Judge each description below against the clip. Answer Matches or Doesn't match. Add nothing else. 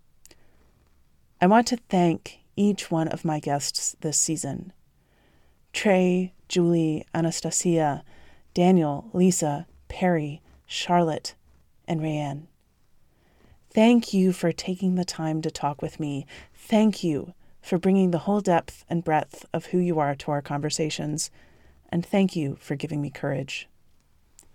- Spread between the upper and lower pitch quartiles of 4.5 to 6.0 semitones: Doesn't match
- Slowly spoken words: Matches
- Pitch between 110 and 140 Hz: Doesn't match